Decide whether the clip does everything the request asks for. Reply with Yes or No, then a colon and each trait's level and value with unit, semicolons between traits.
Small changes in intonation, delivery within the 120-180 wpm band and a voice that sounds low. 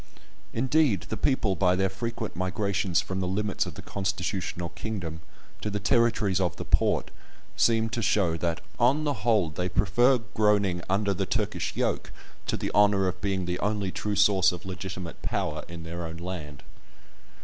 No: average, 3.0 semitones; average, 170 wpm; very low, 95 Hz